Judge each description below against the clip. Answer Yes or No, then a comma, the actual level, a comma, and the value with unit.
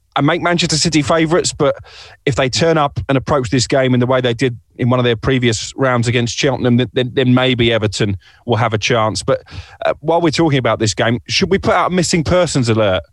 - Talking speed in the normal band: No, fast, 240 wpm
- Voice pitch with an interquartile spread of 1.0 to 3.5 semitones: No, average, 4.0 semitones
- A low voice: Yes, low, 125 Hz